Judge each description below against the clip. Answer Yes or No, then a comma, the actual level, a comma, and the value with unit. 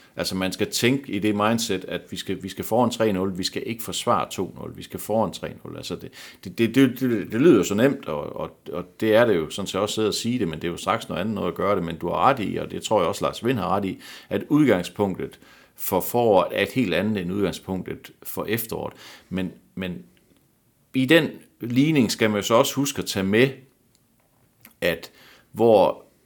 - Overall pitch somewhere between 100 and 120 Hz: Yes, low, 105 Hz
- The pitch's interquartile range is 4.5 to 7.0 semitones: Yes, average, 5.0 semitones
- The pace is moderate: No, fast, 230 wpm